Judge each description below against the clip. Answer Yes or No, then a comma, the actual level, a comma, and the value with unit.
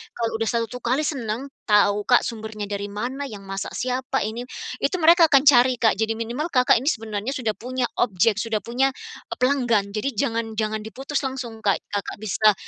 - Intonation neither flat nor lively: Yes, average, 3.3 semitones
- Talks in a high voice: Yes, high, 230 Hz